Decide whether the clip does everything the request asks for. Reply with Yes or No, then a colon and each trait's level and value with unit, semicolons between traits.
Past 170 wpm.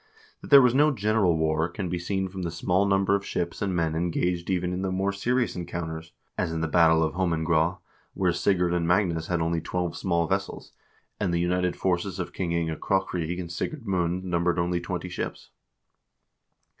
Yes: average, 195 wpm